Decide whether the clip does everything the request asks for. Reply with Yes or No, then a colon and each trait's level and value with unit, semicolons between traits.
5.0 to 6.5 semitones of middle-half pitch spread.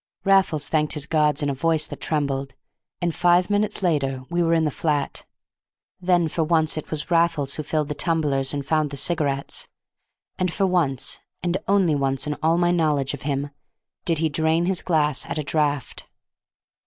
No: average, 3.0 semitones